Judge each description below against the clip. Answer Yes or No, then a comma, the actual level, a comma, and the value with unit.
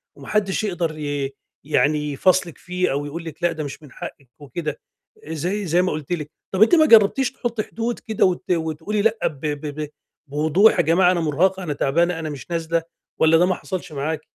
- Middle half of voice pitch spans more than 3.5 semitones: Yes, average, 3.9 semitones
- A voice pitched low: No, medium, 165 Hz